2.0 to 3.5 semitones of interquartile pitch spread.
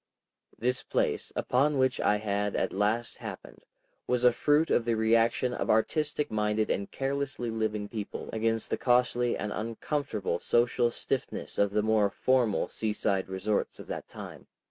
Yes: average, 2.9 semitones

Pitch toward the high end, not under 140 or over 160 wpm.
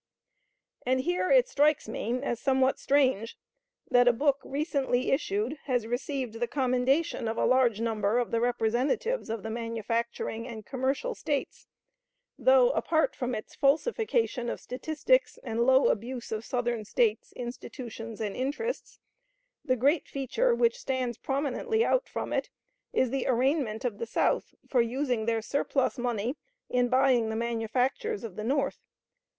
Yes: very high, 255 Hz; average, 150 wpm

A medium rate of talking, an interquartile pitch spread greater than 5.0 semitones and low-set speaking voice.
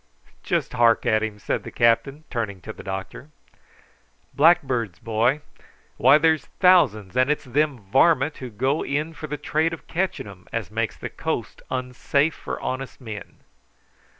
Yes: average, 155 wpm; wide, 5.4 semitones; low, 130 Hz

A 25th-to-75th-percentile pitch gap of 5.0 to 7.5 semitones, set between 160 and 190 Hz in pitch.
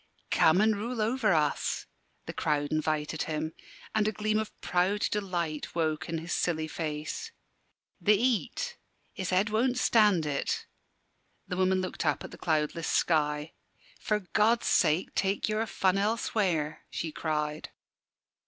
Yes: wide, 5.4 semitones; medium, 185 Hz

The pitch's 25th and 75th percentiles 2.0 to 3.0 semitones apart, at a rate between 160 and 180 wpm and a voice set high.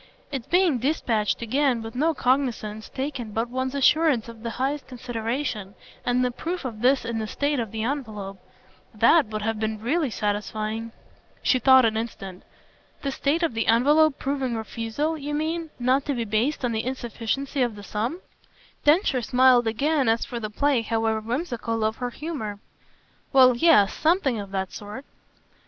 No: average, 4.1 semitones; average, 170 wpm; high, 245 Hz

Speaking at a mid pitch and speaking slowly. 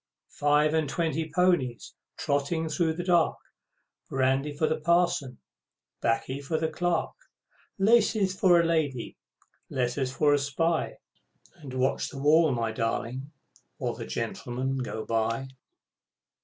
Yes: medium, 145 Hz; slow, 130 wpm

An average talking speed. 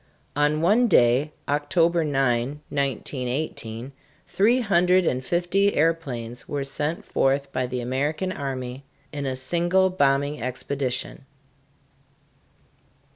No: slow, 105 wpm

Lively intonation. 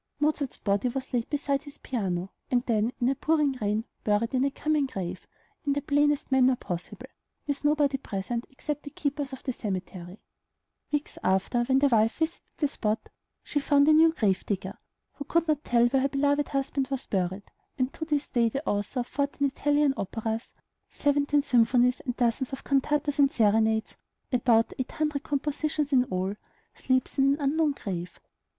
No: average, 4.4 semitones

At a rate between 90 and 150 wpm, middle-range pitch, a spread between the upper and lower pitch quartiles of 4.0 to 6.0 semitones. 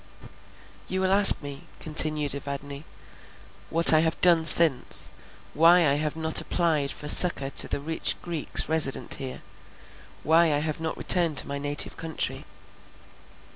No: average, 145 wpm; medium, 155 Hz; narrow, 2.6 semitones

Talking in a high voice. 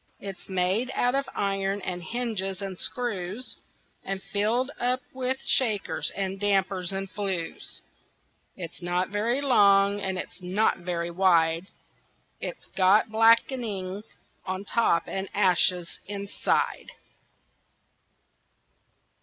Yes: high, 195 Hz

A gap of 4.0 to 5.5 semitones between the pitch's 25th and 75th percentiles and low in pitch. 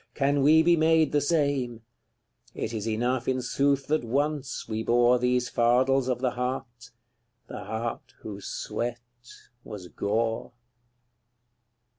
No: average, 3.2 semitones; low, 125 Hz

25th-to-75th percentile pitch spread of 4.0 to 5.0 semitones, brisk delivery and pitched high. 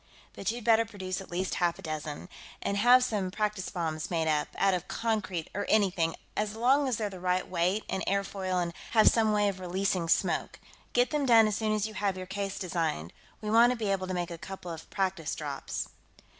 No: average, 3.3 semitones; fast, 220 wpm; high, 195 Hz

